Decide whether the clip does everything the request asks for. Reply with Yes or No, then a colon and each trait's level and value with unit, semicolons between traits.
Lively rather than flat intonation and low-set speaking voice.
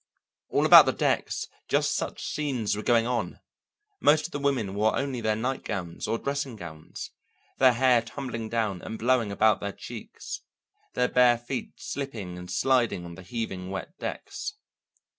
No: average, 4.3 semitones; low, 115 Hz